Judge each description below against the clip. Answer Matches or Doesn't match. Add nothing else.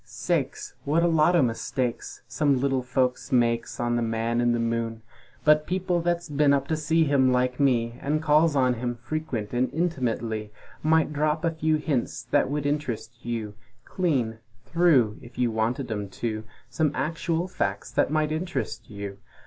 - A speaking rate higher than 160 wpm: Matches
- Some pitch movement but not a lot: Matches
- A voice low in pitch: Matches